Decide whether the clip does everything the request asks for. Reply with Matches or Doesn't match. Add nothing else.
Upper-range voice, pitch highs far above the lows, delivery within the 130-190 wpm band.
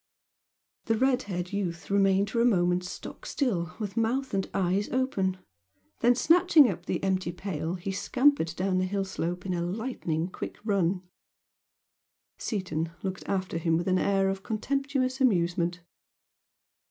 Doesn't match